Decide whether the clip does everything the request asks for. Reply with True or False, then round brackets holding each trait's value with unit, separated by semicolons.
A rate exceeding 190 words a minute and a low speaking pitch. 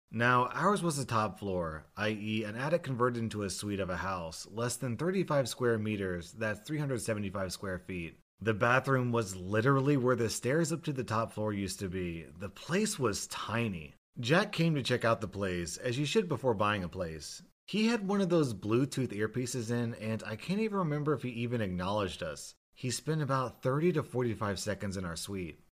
True (200 wpm; 115 Hz)